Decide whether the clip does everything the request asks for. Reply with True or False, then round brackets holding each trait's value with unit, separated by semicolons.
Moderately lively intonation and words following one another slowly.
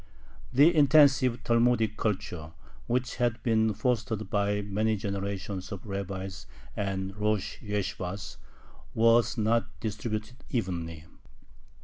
True (3.1 semitones; 100 wpm)